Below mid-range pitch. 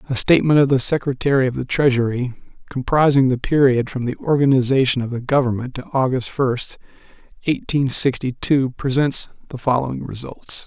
Yes: low, 130 Hz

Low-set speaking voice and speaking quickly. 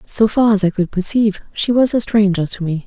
No: high, 205 Hz; fast, 250 wpm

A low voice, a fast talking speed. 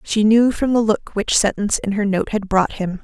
No: high, 210 Hz; fast, 255 wpm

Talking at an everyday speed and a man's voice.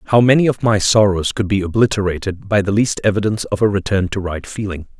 No: fast, 215 wpm; male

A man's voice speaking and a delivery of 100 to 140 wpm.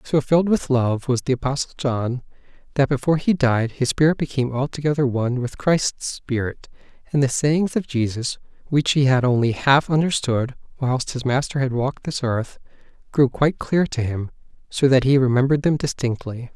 No: male; average, 180 wpm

